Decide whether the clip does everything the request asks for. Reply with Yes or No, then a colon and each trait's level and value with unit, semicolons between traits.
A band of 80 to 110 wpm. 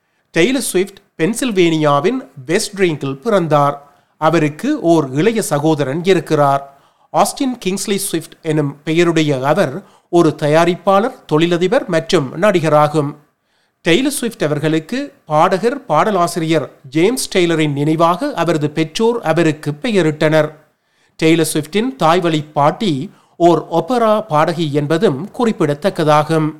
Yes: average, 95 wpm